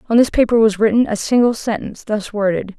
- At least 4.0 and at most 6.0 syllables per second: No, 6.2 syllables/s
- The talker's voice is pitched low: No, high, 200 Hz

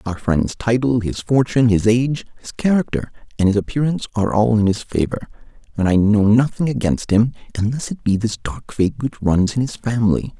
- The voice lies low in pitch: Yes, low, 115 Hz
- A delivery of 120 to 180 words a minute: No, average, 195 wpm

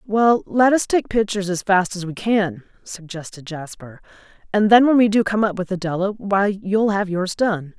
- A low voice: No, high, 200 Hz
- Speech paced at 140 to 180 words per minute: No, average, 200 wpm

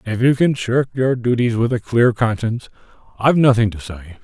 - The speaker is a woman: No, male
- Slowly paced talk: No, average, 200 wpm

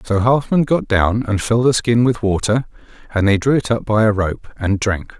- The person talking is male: Yes, male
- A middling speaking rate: No, fast, 230 wpm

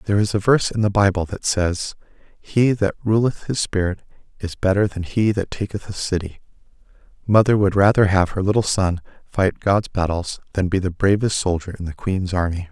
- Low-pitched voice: Yes, very low, 95 Hz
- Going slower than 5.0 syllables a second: No, 5.3 syllables/s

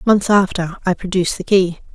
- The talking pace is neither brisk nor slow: Yes, average, 185 wpm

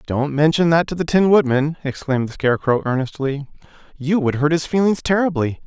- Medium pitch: Yes, medium, 150 Hz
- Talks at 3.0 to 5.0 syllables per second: No, 5.7 syllables/s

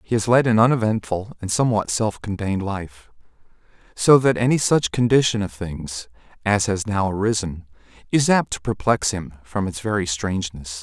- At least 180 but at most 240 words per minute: No, average, 160 wpm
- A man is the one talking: Yes, male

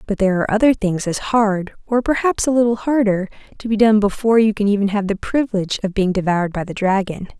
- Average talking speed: No, fast, 225 wpm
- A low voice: No, high, 210 Hz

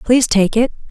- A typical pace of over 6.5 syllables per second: No, 6.2 syllables/s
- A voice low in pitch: No, high, 230 Hz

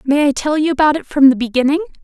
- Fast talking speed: Yes, fast, 265 wpm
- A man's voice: No, female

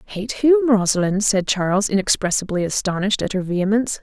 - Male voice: No, female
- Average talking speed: Yes, average, 150 wpm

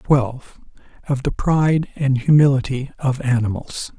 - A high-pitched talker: No, low, 135 Hz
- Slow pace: Yes, slow, 120 wpm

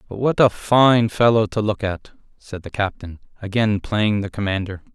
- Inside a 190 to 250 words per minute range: No, average, 180 wpm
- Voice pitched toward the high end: No, low, 105 Hz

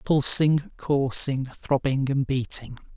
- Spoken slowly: Yes, slow, 100 wpm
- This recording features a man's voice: Yes, male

